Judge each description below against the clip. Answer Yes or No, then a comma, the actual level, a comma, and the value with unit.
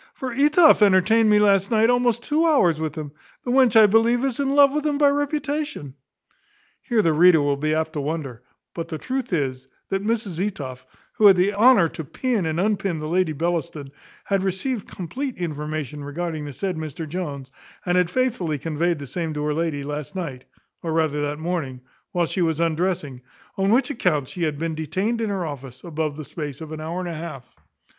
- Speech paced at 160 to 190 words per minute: No, fast, 205 wpm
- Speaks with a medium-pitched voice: Yes, medium, 170 Hz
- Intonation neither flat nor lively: No, wide, 6.2 semitones